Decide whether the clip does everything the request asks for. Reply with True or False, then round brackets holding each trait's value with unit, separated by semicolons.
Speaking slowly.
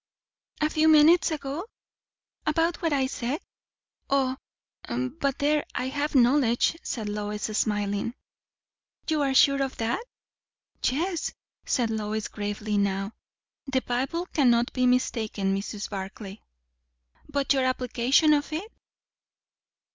True (115 wpm)